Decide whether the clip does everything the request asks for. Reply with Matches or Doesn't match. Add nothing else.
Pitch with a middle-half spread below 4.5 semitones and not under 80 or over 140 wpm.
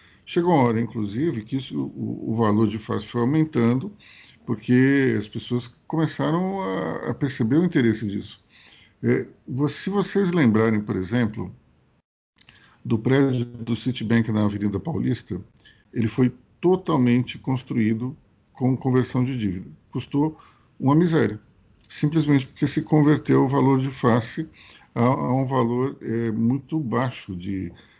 Matches